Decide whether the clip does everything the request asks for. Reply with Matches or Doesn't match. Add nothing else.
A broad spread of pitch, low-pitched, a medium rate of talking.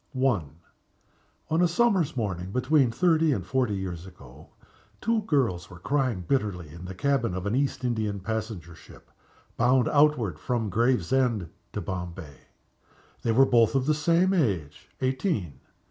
Matches